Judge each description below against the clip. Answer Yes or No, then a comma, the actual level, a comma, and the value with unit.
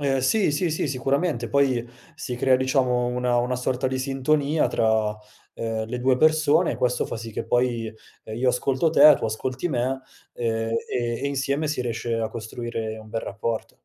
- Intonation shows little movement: No, average, 3.1 semitones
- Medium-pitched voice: No, low, 125 Hz